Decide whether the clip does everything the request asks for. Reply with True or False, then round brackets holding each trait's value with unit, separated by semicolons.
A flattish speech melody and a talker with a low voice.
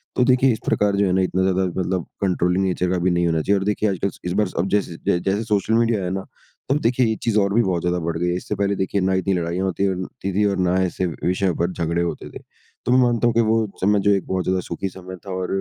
True (2.3 semitones; 95 Hz)